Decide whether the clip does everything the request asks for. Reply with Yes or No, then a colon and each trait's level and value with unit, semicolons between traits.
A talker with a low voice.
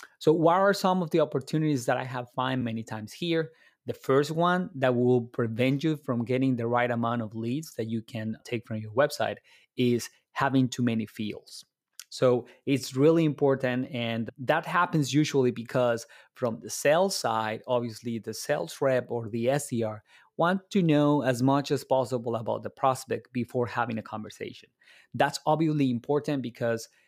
Yes: low, 130 Hz